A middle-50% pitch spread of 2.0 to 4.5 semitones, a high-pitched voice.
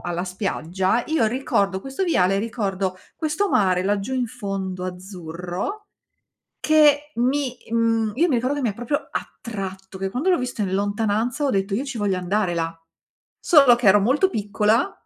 No: wide, 5.5 semitones; high, 215 Hz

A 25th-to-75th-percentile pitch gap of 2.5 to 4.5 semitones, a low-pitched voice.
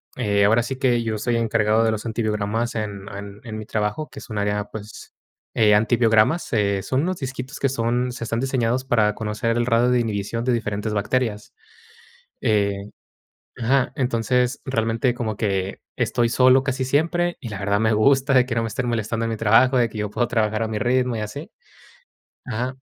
Yes: average, 3.0 semitones; low, 115 Hz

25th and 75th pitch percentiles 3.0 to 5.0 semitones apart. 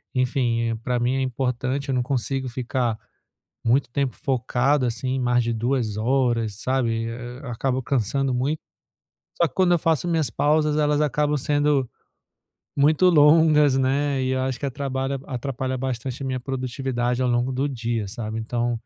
No: narrow, 2.5 semitones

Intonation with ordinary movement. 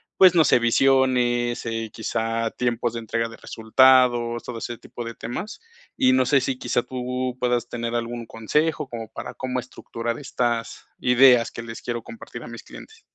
No: narrow, 1.7 semitones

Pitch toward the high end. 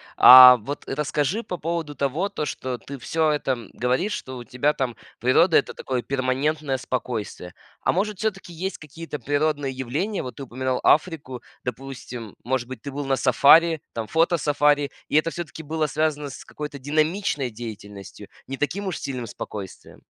No: medium, 140 Hz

